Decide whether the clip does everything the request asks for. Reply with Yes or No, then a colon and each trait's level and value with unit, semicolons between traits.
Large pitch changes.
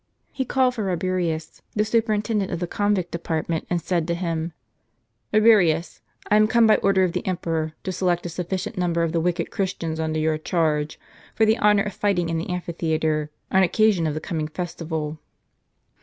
No: average, 3.7 semitones